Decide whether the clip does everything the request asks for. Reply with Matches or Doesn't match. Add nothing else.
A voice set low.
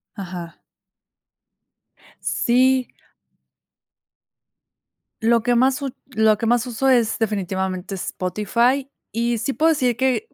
Doesn't match